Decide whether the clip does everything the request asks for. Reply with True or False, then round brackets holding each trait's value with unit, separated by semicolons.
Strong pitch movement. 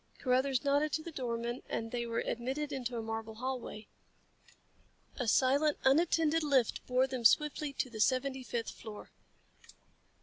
False (3.2 semitones)